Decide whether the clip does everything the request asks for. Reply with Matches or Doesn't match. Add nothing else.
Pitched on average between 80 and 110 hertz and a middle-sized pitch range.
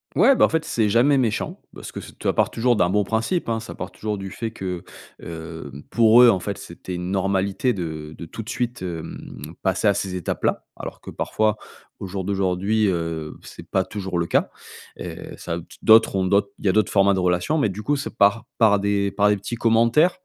Matches